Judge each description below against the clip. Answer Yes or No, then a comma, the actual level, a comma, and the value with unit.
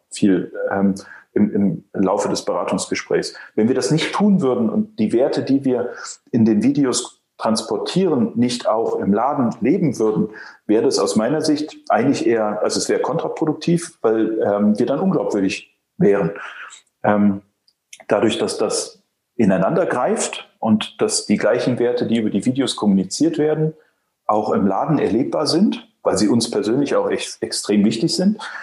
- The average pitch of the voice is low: Yes, low, 120 Hz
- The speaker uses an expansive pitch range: Yes, wide, 7.0 semitones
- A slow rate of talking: No, average, 160 wpm